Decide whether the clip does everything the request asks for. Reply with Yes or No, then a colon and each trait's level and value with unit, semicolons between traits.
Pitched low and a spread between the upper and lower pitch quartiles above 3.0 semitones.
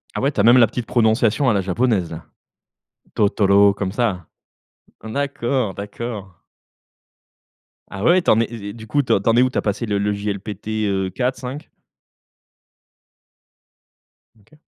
Yes: low, 110 Hz; average, 3.5 semitones